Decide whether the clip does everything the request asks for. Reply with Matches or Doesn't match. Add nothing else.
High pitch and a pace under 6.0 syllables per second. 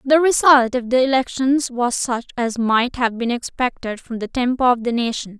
Matches